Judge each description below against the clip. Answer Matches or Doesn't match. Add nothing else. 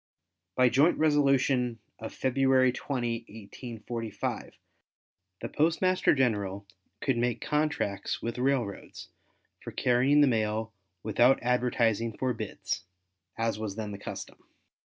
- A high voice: Doesn't match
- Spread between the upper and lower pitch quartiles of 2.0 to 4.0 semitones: Matches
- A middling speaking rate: Doesn't match